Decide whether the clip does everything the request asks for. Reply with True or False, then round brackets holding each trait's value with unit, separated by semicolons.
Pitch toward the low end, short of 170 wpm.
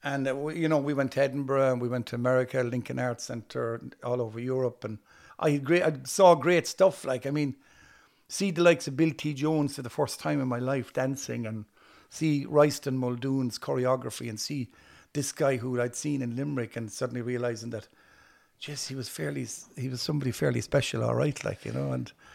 False (130 Hz; 205 wpm)